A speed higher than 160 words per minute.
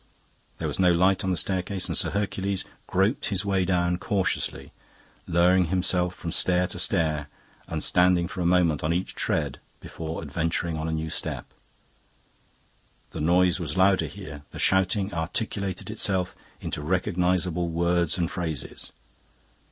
No: average, 150 wpm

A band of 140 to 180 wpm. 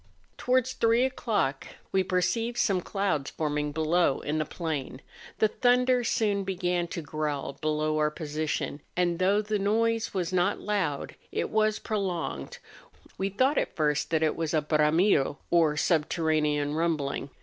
Yes: average, 150 wpm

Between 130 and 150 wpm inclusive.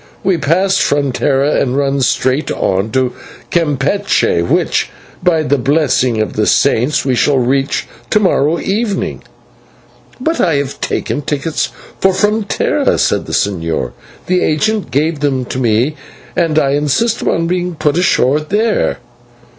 Yes: average, 145 wpm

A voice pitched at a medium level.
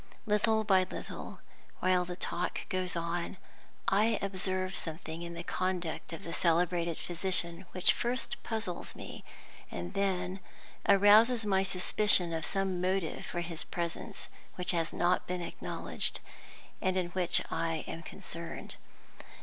Yes: medium, 180 Hz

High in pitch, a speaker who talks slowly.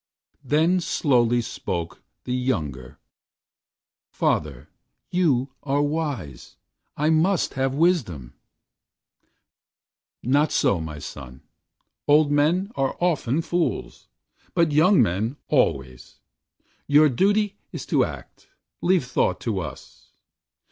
No: medium, 140 Hz; slow, 100 wpm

